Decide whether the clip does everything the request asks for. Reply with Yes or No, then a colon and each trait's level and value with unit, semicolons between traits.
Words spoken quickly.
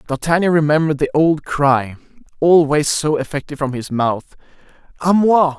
No: average, 140 wpm